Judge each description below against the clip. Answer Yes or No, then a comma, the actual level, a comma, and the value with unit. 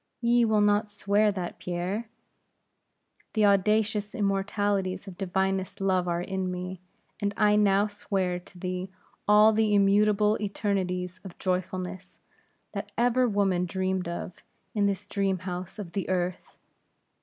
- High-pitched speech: Yes, high, 195 Hz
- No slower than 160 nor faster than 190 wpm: No, slow, 135 wpm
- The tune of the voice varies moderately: No, narrow, 2.1 semitones